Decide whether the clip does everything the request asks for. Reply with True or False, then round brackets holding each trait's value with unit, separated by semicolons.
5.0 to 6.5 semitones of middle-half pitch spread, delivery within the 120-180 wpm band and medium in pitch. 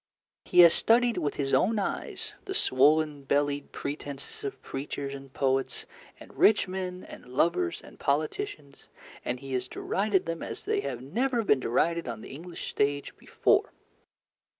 True (5.3 semitones; 155 wpm; 145 Hz)